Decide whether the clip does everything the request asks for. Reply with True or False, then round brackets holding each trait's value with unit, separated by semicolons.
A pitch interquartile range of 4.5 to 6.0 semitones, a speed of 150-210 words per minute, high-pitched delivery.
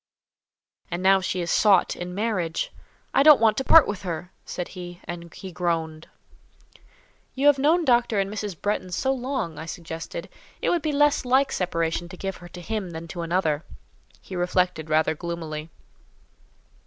False (4.8 semitones; 170 wpm; 180 Hz)